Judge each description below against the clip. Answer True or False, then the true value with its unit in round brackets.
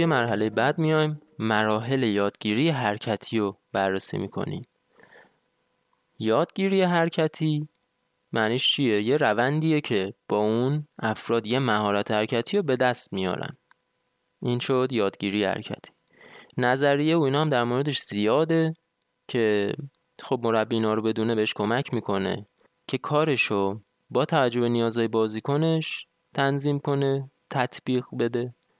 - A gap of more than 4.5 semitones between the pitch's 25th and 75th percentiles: True (5.4 semitones)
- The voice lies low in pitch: True (125 Hz)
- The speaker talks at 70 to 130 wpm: True (120 wpm)